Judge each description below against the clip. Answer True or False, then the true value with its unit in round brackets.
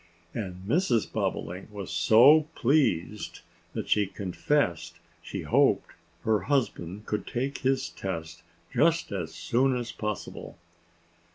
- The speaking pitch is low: True (105 Hz)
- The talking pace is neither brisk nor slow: False (115 wpm)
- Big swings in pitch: True (6.4 semitones)